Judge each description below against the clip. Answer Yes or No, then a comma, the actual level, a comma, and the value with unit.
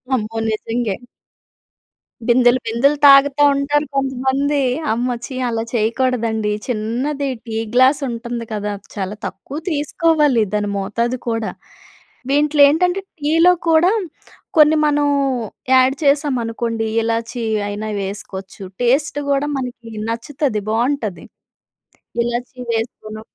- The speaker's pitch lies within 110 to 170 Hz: No, high, 245 Hz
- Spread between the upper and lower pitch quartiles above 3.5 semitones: Yes, average, 4.1 semitones